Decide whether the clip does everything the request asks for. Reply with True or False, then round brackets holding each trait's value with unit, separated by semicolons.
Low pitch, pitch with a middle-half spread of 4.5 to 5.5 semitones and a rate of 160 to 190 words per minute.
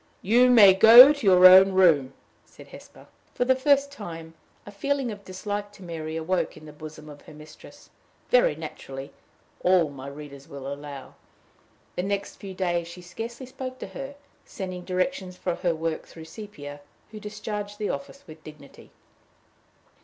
False (185 Hz; 5.2 semitones; 165 wpm)